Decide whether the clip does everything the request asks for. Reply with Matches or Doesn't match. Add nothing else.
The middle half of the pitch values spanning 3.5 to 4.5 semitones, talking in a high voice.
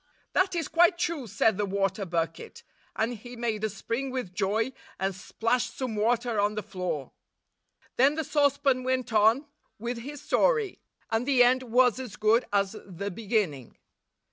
Matches